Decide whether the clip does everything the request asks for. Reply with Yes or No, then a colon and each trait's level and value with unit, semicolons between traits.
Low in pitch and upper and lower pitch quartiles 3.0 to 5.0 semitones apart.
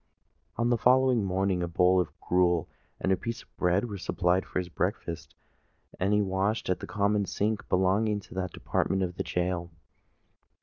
No: very low, 95 Hz; narrow, 2.6 semitones